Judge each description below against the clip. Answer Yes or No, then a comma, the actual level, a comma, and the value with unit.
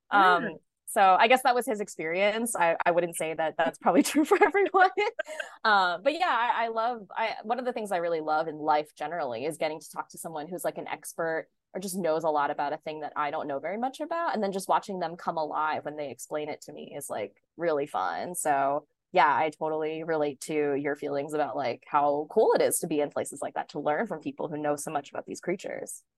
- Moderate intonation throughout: No, wide, 6.9 semitones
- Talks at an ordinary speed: No, fast, 250 wpm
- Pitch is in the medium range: Yes, medium, 165 Hz